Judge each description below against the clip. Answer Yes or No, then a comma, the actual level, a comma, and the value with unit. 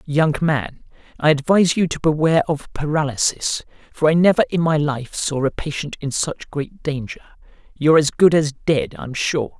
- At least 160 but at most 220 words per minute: Yes, average, 180 wpm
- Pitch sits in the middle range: Yes, medium, 150 Hz